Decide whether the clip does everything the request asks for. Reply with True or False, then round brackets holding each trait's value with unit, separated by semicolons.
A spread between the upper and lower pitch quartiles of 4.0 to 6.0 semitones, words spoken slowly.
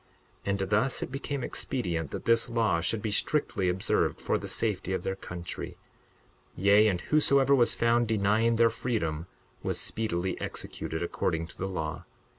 False (4.6 semitones; 165 wpm)